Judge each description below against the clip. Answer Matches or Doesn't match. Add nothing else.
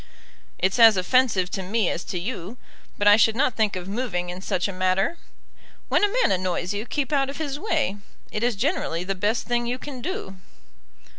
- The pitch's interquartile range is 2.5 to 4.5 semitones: Doesn't match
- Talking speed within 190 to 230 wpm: Matches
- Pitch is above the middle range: Matches